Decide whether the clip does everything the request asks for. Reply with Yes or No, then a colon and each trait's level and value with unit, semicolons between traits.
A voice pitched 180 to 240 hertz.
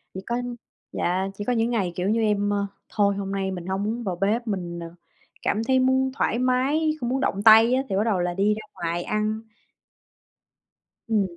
Yes: high, 210 Hz